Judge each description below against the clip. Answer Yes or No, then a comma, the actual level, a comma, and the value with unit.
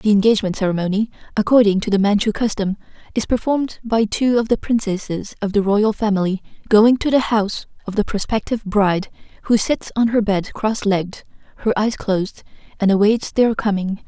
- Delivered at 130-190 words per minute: Yes, average, 175 wpm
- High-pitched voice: Yes, high, 210 Hz